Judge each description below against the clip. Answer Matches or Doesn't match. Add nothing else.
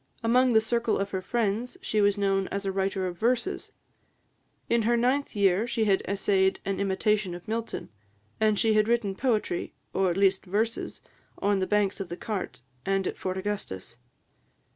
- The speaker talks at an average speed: Matches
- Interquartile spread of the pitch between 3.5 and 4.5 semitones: Doesn't match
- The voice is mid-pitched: Doesn't match